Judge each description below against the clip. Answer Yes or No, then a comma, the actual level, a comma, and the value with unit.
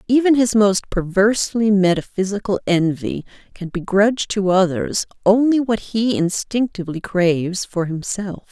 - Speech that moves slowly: Yes, slow, 120 wpm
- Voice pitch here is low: No, high, 200 Hz